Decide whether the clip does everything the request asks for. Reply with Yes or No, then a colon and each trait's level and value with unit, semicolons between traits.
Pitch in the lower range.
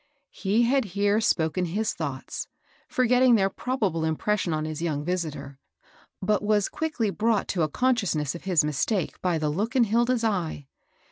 No: high, 195 Hz